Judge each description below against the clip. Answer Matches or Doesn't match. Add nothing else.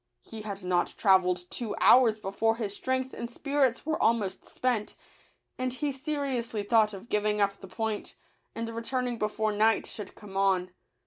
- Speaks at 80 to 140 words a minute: Doesn't match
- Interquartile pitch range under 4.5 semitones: Matches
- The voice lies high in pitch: Matches